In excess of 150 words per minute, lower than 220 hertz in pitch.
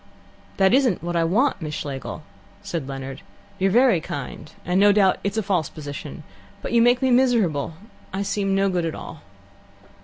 Yes: average, 180 wpm; high, 190 Hz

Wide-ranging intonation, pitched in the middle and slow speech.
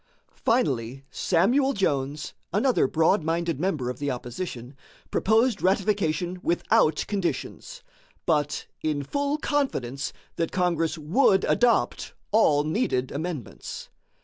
Yes: wide, 6.3 semitones; medium, 170 Hz; slow, 105 wpm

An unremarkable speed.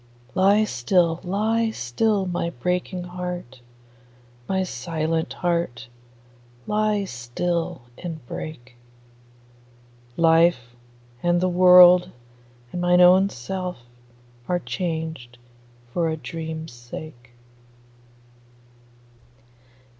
No: slow, 85 wpm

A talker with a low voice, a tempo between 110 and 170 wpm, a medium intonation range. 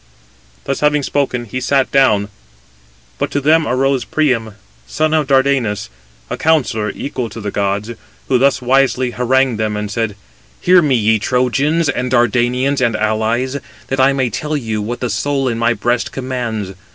Yes: low, 125 Hz; average, 165 wpm; average, 3.5 semitones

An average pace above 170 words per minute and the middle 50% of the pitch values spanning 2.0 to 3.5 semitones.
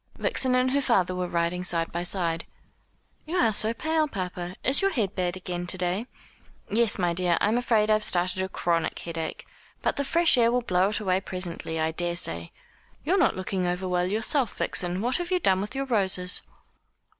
No: average, 195 wpm; average, 5.0 semitones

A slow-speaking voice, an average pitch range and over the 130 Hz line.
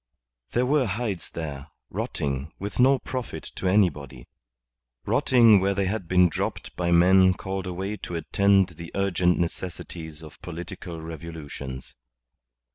No: slow, 130 wpm; average, 3.4 semitones; very low, 90 Hz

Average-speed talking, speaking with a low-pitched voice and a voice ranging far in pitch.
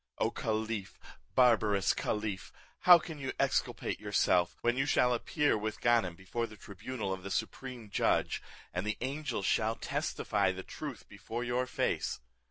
No: average, 155 wpm; low, 110 Hz; average, 4.1 semitones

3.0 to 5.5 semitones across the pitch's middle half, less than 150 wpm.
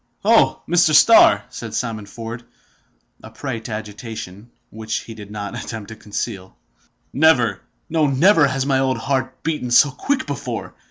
No: average, 4.1 semitones; average, 155 wpm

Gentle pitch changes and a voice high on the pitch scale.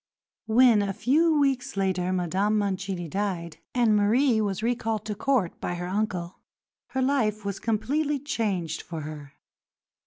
No: average, 4.9 semitones; high, 210 Hz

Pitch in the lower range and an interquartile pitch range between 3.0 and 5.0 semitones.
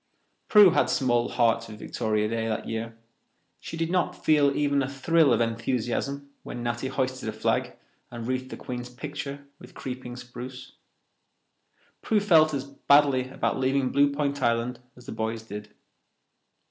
Yes: low, 130 Hz; average, 3.4 semitones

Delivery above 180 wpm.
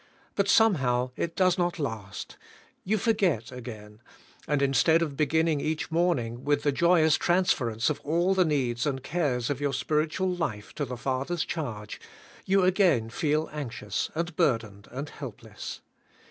No: average, 155 wpm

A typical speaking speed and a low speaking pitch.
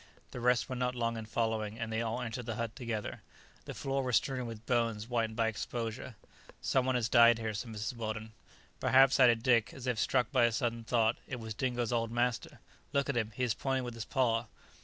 No: fast, 225 wpm; low, 115 Hz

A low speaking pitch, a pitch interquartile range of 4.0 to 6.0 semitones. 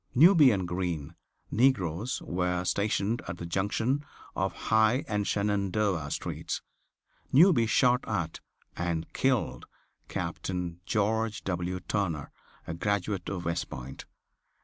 Yes: low, 100 Hz; average, 4.3 semitones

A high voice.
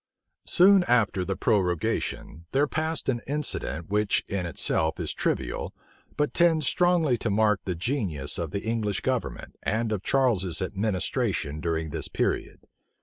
No: low, 105 Hz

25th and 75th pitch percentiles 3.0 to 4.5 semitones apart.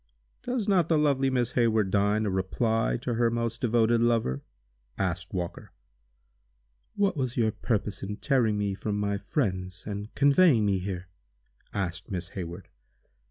Yes: average, 4.0 semitones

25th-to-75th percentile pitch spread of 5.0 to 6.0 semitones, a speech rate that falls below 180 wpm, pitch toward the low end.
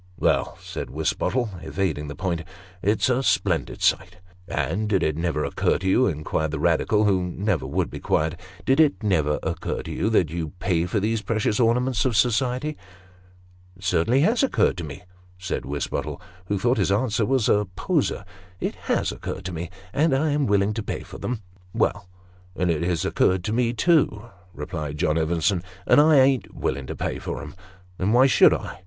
No: wide, 5.6 semitones; fast, 205 wpm; very low, 95 Hz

